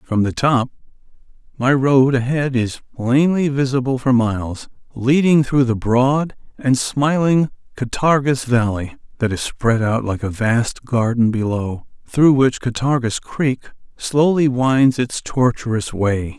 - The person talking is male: Yes, male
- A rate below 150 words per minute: Yes, slow, 135 wpm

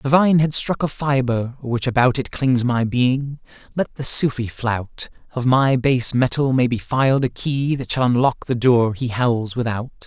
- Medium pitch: No, low, 125 Hz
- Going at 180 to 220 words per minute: Yes, average, 190 wpm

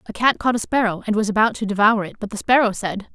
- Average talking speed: No, fast, 285 wpm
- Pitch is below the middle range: No, high, 215 Hz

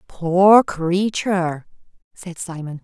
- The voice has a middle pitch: Yes, medium, 180 Hz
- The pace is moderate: No, slow, 85 wpm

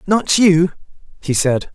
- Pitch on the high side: No, medium, 170 Hz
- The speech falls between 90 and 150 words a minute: Yes, average, 140 wpm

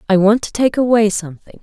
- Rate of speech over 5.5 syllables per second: Yes, 6.3 syllables/s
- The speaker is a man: No, female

